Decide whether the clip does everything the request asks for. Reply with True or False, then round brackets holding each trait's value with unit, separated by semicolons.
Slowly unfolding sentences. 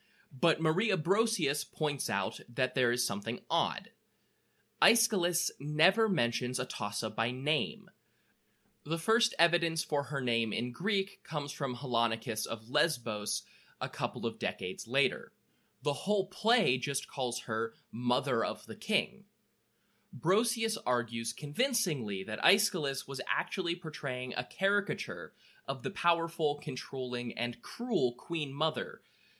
True (125 wpm)